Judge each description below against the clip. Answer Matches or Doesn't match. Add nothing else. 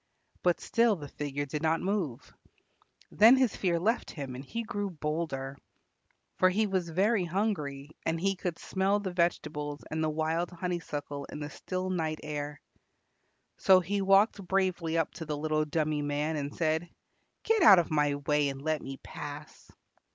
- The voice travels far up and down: Doesn't match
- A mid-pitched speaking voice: Matches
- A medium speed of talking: Matches